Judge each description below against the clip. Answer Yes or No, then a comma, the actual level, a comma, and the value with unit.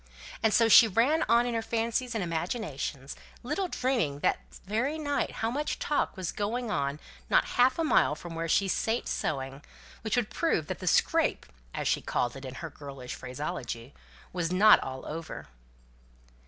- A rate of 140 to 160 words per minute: No, average, 175 wpm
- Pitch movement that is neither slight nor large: No, wide, 8.7 semitones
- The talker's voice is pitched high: Yes, high, 195 Hz